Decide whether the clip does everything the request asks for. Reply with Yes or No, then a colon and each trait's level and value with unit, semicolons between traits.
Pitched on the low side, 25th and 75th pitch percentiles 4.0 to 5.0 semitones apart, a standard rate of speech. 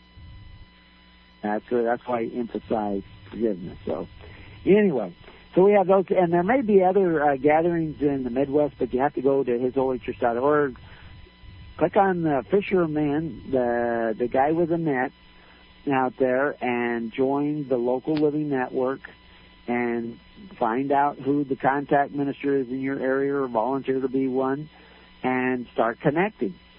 Yes: low, 130 Hz; average, 4.3 semitones; average, 150 wpm